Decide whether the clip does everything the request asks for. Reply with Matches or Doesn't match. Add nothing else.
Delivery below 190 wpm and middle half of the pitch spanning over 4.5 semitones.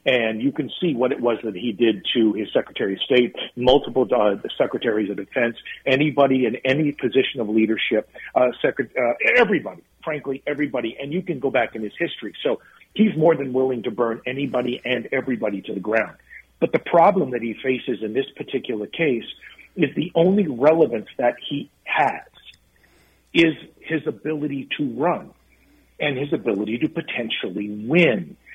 Matches